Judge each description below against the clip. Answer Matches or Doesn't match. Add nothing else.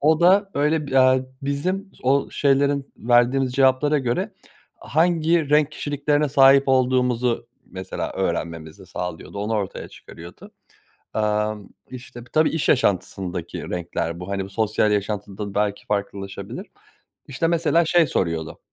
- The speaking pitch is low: Matches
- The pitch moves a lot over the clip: Matches